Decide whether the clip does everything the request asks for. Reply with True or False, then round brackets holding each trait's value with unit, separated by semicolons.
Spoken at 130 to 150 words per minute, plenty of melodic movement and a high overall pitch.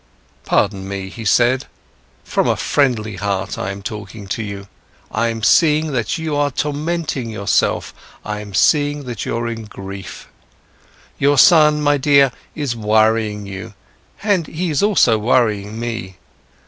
False (135 wpm; 5.8 semitones; 115 Hz)